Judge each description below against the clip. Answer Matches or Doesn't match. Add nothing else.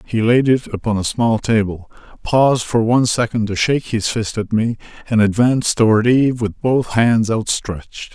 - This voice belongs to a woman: Doesn't match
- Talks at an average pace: Matches